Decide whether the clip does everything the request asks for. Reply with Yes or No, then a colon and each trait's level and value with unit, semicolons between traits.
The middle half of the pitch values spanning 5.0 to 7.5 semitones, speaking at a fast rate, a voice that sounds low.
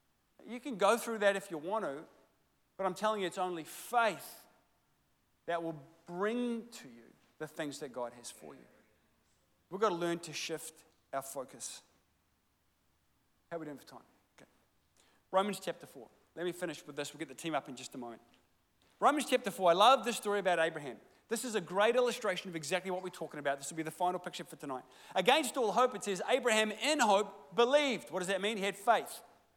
No: wide, 5.6 semitones; fast, 210 wpm; medium, 180 Hz